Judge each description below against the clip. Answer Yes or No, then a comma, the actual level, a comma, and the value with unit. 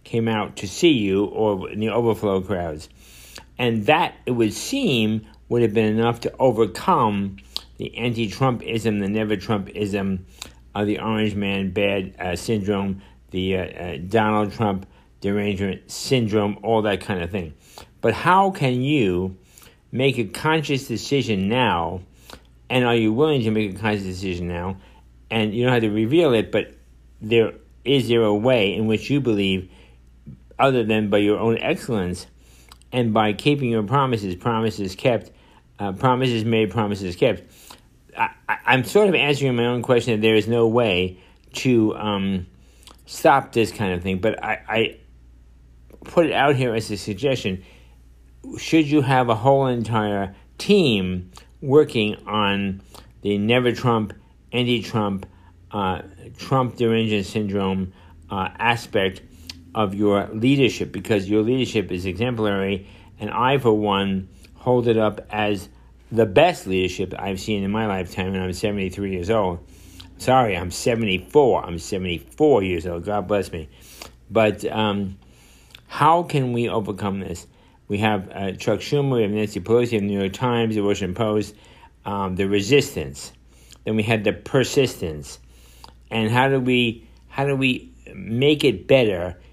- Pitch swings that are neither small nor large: Yes, average, 3.7 semitones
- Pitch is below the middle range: Yes, low, 105 Hz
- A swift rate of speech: No, average, 155 wpm